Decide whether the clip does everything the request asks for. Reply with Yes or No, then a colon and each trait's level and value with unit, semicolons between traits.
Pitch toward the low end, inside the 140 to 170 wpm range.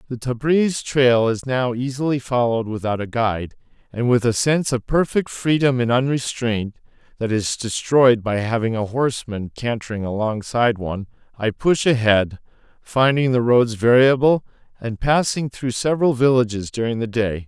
Yes: low, 120 Hz; average, 150 wpm